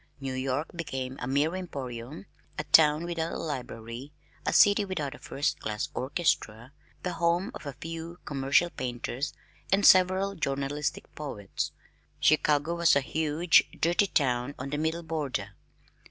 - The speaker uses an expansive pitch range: No, average, 4.2 semitones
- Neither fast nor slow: Yes, average, 145 wpm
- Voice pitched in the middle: Yes, medium, 150 Hz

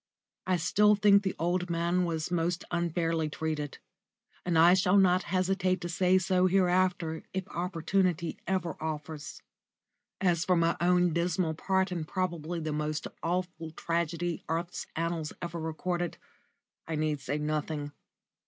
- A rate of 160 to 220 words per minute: No, average, 140 wpm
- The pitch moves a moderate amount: No, narrow, 2.2 semitones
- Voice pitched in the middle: Yes, medium, 175 Hz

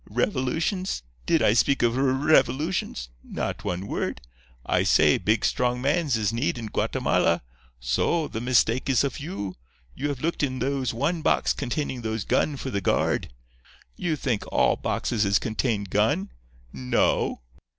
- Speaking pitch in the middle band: No, low, 125 Hz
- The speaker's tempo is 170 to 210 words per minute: No, average, 160 wpm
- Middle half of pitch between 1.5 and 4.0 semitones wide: No, average, 4.6 semitones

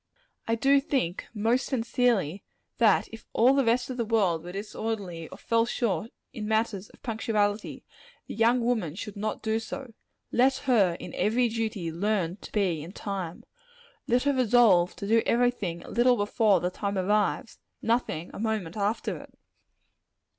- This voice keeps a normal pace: Yes, average, 170 wpm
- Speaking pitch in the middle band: No, high, 220 Hz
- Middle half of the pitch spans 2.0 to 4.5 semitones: Yes, average, 3.5 semitones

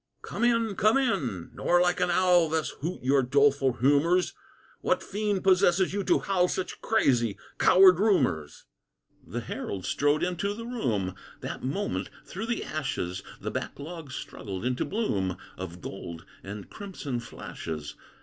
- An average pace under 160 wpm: Yes, average, 150 wpm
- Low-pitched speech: No, medium, 160 Hz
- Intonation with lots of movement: Yes, wide, 8.4 semitones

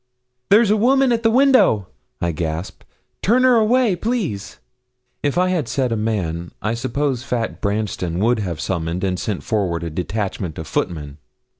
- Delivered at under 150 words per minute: No, average, 165 wpm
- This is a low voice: Yes, low, 110 Hz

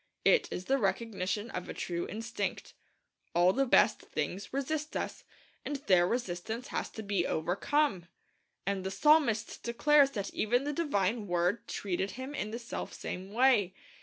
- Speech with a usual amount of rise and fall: No, wide, 5.8 semitones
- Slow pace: No, average, 155 wpm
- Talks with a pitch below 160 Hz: No, high, 220 Hz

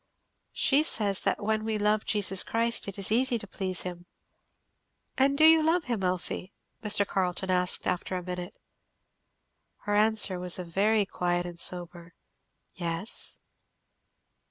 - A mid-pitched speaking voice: No, high, 195 Hz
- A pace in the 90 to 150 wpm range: Yes, average, 145 wpm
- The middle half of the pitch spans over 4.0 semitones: No, average, 3.4 semitones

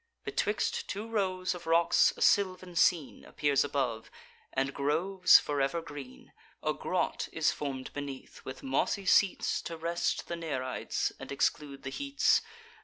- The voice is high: No, medium, 160 Hz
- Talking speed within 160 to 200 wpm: No, average, 145 wpm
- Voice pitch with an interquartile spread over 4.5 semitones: Yes, average, 5.1 semitones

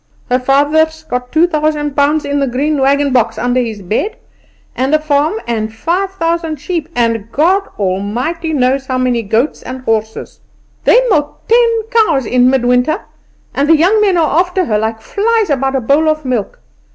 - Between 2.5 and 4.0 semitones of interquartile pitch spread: No, average, 4.7 semitones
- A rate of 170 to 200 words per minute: Yes, average, 180 wpm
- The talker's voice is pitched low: No, very high, 285 Hz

